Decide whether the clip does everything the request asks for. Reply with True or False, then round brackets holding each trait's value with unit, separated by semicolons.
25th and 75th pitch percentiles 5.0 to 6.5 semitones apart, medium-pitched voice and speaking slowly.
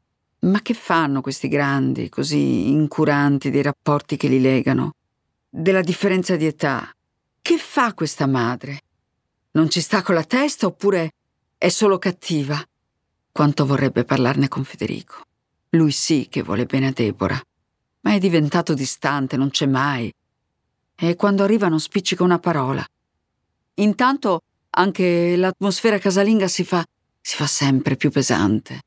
False (5.6 semitones; 150 Hz; 140 wpm)